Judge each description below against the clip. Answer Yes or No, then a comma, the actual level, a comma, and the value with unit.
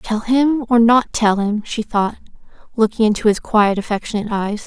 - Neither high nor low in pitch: No, high, 220 Hz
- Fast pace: No, average, 180 wpm